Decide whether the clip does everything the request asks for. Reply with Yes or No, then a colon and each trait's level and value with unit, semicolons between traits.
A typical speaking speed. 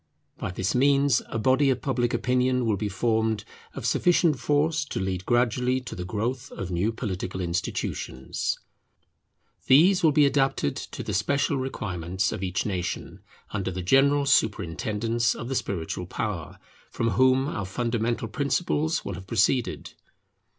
Yes: average, 150 wpm